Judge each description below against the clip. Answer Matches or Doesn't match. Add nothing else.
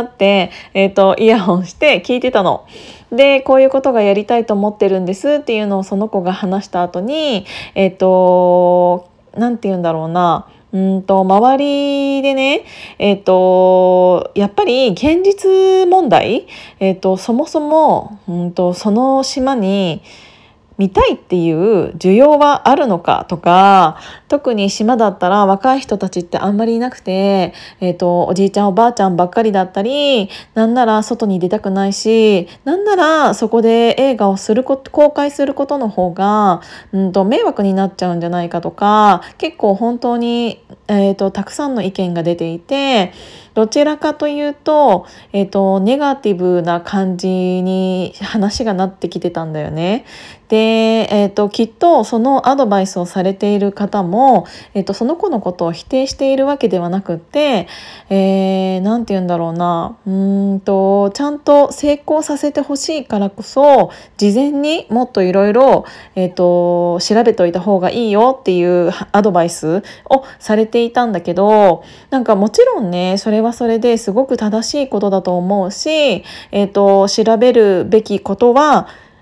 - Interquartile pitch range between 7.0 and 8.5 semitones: Doesn't match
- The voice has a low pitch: Doesn't match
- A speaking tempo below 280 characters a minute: Doesn't match